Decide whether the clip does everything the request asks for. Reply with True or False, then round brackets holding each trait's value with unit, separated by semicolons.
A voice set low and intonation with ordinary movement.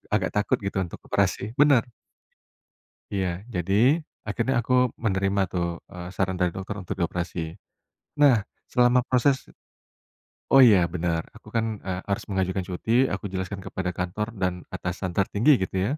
True (95 Hz; 3.7 semitones)